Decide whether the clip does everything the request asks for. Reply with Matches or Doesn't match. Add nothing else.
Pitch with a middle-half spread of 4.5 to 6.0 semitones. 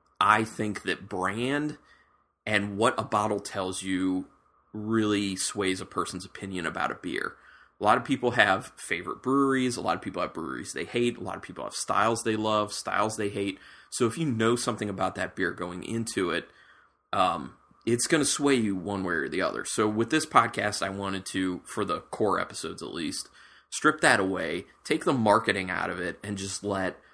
Doesn't match